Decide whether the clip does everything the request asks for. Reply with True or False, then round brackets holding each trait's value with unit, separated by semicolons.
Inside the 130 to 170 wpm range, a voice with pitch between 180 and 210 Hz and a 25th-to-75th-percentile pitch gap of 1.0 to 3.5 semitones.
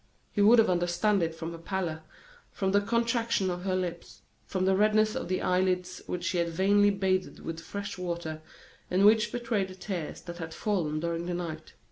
False (195 wpm; 185 Hz; 2.9 semitones)